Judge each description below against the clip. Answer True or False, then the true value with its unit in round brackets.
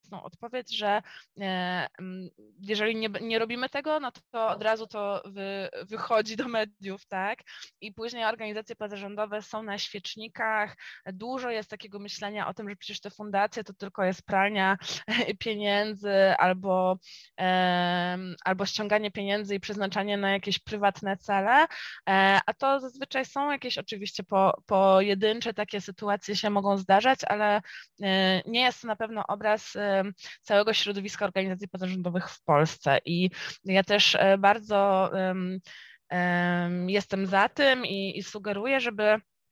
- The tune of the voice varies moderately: False (2.0 semitones)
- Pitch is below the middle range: False (205 Hz)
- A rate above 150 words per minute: False (135 wpm)